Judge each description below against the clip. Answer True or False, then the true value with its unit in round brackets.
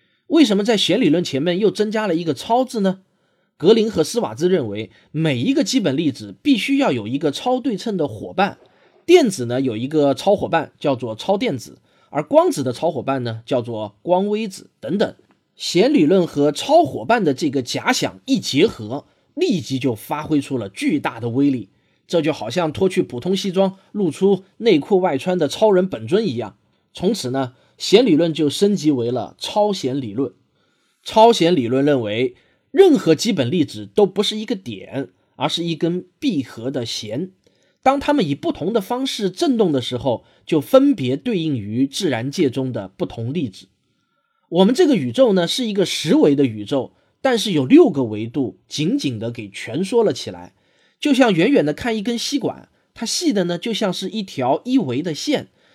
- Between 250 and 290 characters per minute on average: True (265 characters per minute)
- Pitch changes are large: True (9.0 semitones)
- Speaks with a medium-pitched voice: True (175 Hz)